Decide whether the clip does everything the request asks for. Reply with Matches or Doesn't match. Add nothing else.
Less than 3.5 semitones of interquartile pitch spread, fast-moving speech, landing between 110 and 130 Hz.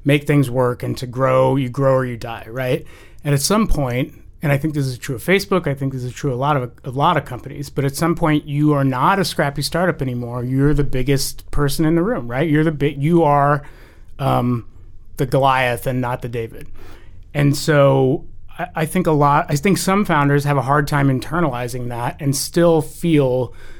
Doesn't match